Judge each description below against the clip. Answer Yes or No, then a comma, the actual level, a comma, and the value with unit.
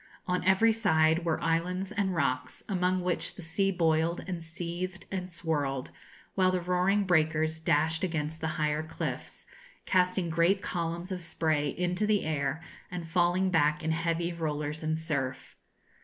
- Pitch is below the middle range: No, medium, 170 Hz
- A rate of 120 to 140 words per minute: No, average, 155 wpm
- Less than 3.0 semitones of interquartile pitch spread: Yes, narrow, 2.4 semitones